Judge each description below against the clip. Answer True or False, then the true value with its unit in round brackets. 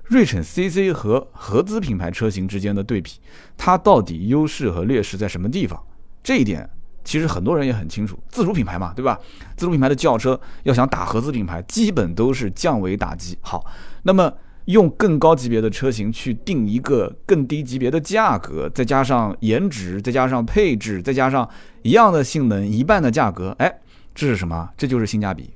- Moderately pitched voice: False (125 Hz)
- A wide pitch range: True (7.3 semitones)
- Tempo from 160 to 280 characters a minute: False (295 characters per minute)